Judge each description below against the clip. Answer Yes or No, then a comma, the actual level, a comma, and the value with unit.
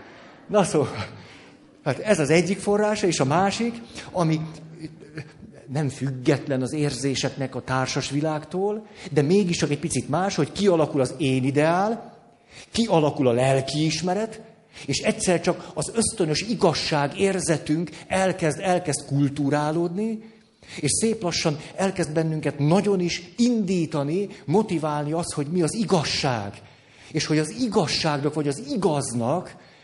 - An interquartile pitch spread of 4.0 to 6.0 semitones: Yes, average, 4.9 semitones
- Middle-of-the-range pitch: Yes, medium, 160 Hz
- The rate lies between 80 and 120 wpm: No, average, 130 wpm